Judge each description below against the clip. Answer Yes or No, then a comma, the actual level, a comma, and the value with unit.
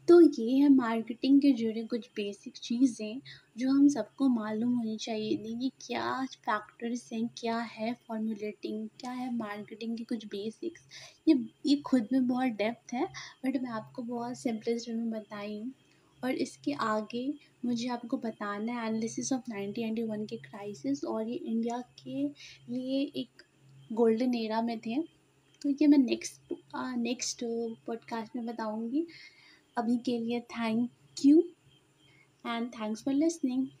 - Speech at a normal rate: Yes, average, 145 wpm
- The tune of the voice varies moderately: Yes, average, 3.0 semitones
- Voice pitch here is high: Yes, high, 235 Hz